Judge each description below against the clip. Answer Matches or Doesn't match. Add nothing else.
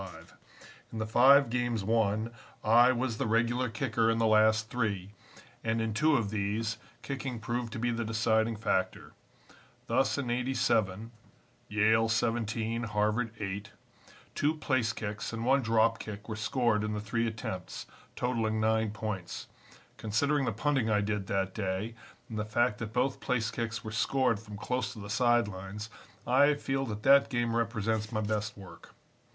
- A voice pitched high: Doesn't match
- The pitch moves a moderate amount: Doesn't match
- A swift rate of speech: Doesn't match